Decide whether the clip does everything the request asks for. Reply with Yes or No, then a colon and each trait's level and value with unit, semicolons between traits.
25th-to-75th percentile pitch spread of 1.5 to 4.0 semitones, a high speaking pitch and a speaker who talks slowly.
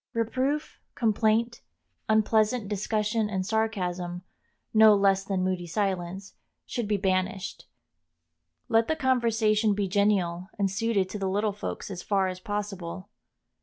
Yes: average, 2.7 semitones; high, 205 Hz; slow, 130 wpm